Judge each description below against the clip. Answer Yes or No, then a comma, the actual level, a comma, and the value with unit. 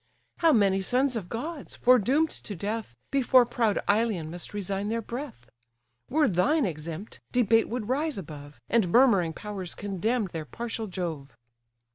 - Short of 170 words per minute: Yes, average, 145 wpm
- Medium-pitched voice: No, high, 215 Hz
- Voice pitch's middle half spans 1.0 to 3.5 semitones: No, wide, 5.5 semitones